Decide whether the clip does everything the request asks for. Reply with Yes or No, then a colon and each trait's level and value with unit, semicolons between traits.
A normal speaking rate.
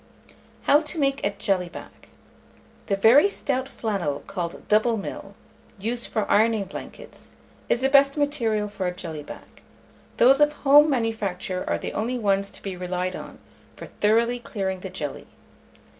Yes: average, 160 wpm